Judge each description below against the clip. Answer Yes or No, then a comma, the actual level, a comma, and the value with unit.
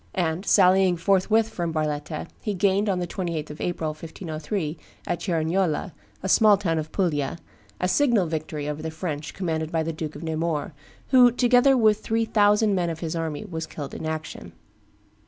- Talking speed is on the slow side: No, average, 175 wpm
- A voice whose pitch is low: No, medium, 170 Hz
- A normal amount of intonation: Yes, average, 4.0 semitones